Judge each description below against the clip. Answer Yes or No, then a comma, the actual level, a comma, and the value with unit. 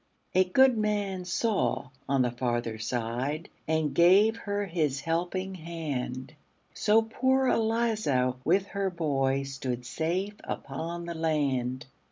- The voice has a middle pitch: Yes, medium, 165 Hz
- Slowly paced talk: Yes, slow, 125 wpm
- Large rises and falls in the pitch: Yes, wide, 6.8 semitones